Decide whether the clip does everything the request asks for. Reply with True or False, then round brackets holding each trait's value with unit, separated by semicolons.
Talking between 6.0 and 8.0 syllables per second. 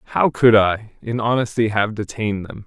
False (5.2 syllables/s)